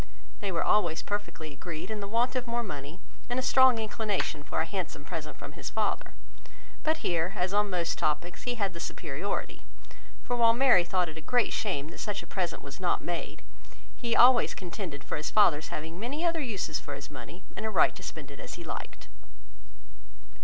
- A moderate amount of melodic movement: No, wide, 6.1 semitones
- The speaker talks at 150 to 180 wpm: No, fast, 205 wpm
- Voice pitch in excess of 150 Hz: Yes, medium, 185 Hz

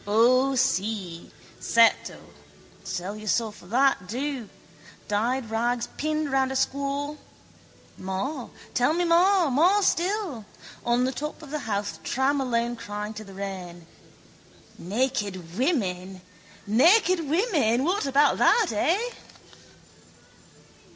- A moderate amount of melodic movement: No, wide, 5.9 semitones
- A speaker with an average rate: No, slow, 115 wpm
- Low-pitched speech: No, very high, 250 Hz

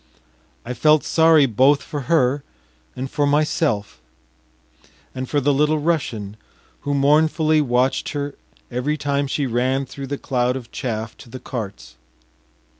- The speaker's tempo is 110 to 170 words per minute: Yes, average, 140 wpm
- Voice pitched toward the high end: No, low, 135 Hz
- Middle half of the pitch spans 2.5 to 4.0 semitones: Yes, average, 3.0 semitones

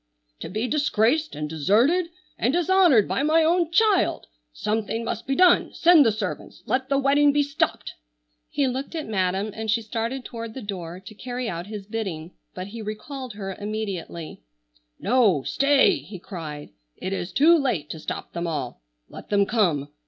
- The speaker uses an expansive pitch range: Yes, wide, 6.6 semitones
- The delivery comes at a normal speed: Yes, average, 175 wpm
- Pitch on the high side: Yes, high, 220 Hz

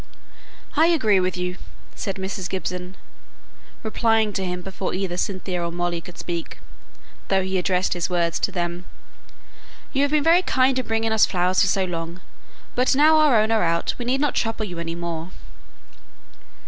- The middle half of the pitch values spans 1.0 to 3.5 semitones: No, average, 4.1 semitones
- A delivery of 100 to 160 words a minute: No, average, 175 wpm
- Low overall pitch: No, high, 190 Hz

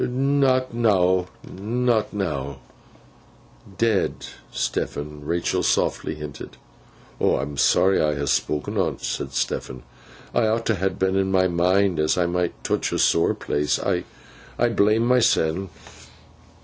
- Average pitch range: No, wide, 6.7 semitones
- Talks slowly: Yes, slow, 125 wpm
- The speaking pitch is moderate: No, very low, 95 Hz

